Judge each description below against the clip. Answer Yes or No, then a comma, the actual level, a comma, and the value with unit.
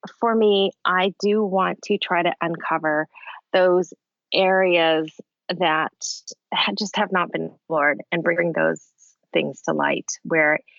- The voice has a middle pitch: Yes, medium, 180 Hz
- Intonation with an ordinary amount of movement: Yes, average, 3.4 semitones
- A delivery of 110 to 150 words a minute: Yes, slow, 135 wpm